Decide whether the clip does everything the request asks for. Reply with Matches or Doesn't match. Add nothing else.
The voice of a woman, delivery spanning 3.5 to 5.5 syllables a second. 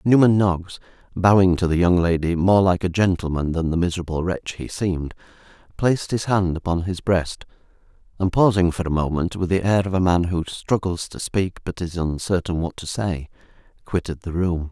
Doesn't match